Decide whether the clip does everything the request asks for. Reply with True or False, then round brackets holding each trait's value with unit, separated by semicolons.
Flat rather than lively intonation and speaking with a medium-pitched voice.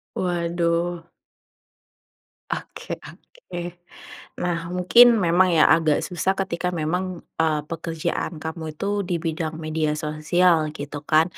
True (2.2 semitones; 170 Hz)